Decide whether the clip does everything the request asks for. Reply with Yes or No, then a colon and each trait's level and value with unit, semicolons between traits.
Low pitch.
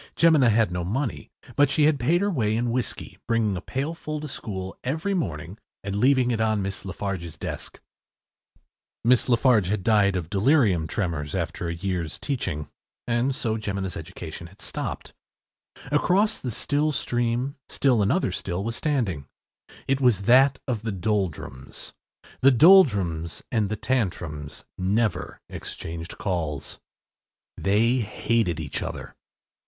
Yes: low, 110 Hz